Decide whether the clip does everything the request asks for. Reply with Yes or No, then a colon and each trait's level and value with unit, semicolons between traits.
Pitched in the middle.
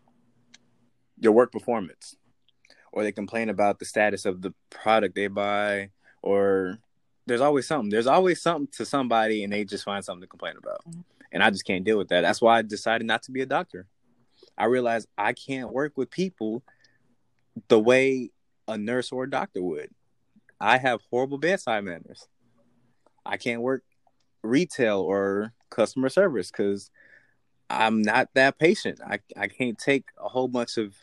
No: low, 115 Hz